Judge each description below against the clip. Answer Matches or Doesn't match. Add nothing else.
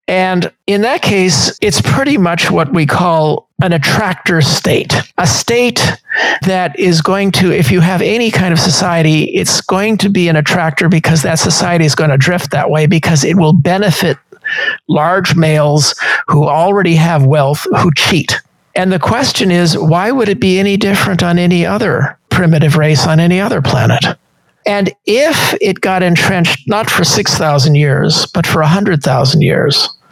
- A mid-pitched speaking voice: Matches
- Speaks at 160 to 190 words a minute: Matches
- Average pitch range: Matches